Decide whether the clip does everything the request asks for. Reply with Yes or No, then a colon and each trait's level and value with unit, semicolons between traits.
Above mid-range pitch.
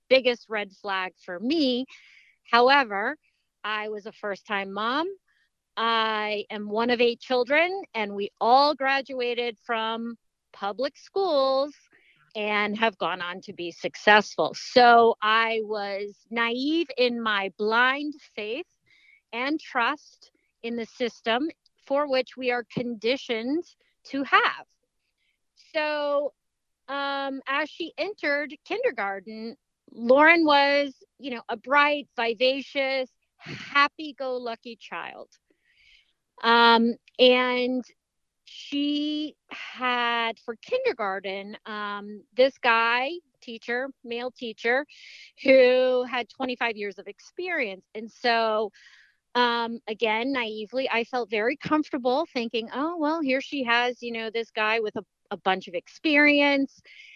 Yes: high, 245 Hz